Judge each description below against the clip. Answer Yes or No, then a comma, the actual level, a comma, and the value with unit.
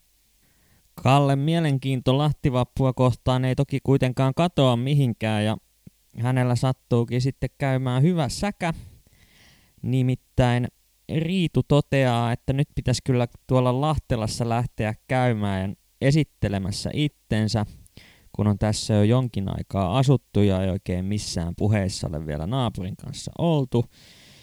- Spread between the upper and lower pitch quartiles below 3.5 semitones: No, average, 4.1 semitones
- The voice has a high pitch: No, low, 125 Hz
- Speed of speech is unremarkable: Yes, average, 115 wpm